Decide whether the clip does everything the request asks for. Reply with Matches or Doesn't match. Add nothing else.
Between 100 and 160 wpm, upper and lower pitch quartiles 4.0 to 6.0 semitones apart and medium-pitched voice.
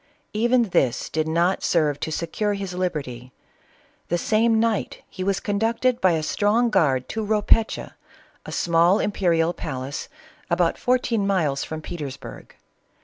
Matches